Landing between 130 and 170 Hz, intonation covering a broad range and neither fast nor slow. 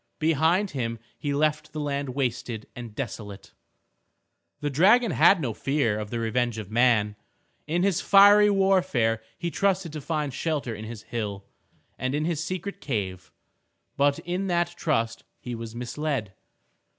Yes: medium, 140 Hz; wide, 6.7 semitones; average, 150 wpm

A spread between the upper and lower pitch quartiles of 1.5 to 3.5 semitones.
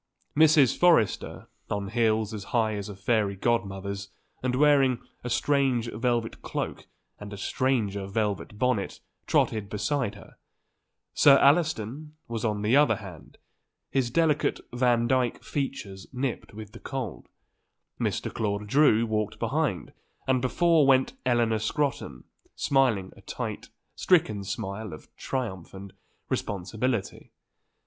No: average, 4.5 semitones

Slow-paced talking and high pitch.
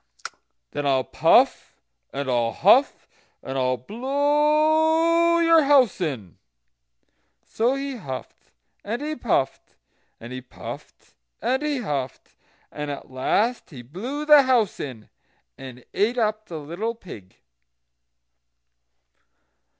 Yes: slow, 115 wpm; high, 215 Hz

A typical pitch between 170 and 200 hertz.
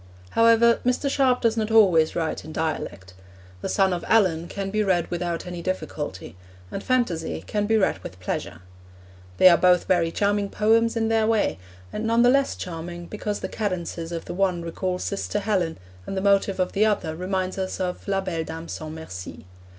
Yes: medium, 185 Hz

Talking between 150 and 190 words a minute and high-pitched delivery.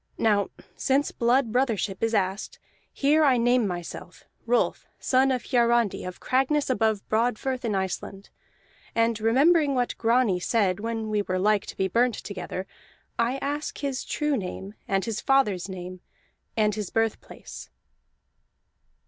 No: average, 140 wpm; high, 225 Hz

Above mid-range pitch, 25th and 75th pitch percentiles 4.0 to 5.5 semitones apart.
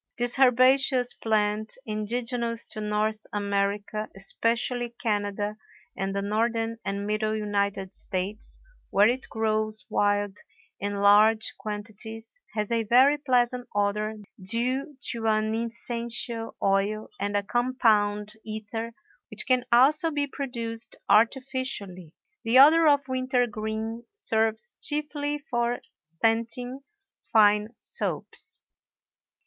No: high, 225 Hz; average, 2.8 semitones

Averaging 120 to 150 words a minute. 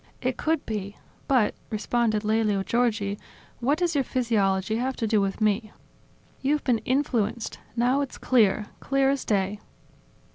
Yes: average, 145 wpm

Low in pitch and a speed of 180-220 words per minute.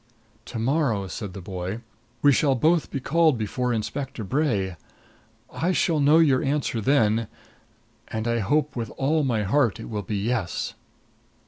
No: low, 125 Hz; average, 155 wpm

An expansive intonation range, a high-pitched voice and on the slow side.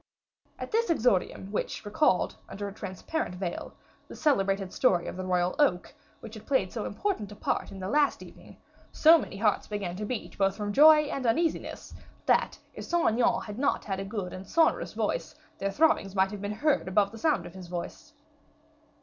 No: wide, 6.9 semitones; high, 205 Hz; average, 195 wpm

